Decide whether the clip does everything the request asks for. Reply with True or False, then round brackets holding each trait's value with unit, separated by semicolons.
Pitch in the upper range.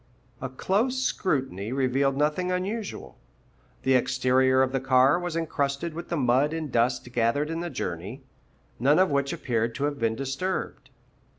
False (135 Hz)